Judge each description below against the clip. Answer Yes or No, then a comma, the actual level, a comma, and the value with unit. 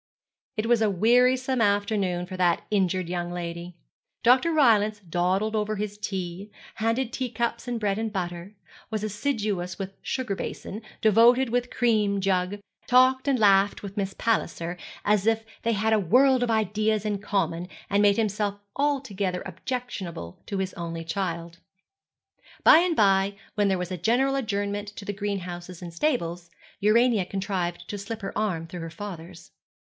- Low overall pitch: No, high, 205 Hz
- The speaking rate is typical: Yes, average, 165 wpm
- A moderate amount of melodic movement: Yes, average, 3.8 semitones